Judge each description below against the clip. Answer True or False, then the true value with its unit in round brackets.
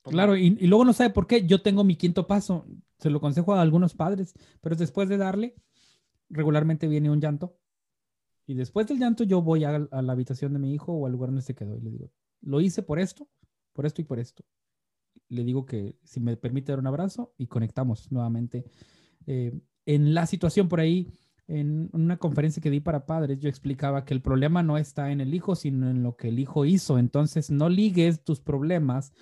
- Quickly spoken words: True (215 wpm)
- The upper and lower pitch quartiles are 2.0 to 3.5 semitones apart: False (4.9 semitones)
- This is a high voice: False (150 Hz)